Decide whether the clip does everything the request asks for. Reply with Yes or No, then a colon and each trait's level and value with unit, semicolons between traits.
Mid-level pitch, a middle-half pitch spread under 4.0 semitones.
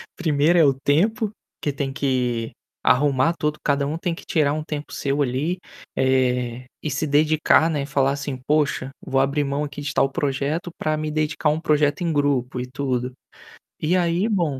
Yes: medium, 145 Hz; narrow, 2.4 semitones